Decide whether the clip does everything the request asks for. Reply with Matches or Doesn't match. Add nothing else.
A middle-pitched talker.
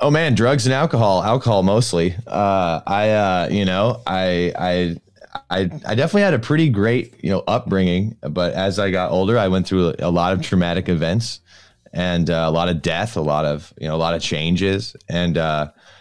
Doesn't match